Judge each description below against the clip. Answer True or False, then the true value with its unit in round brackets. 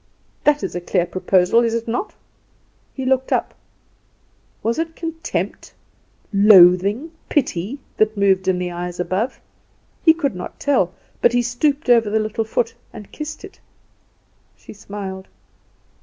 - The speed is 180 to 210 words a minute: False (140 wpm)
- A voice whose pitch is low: False (220 Hz)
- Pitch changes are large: True (6.7 semitones)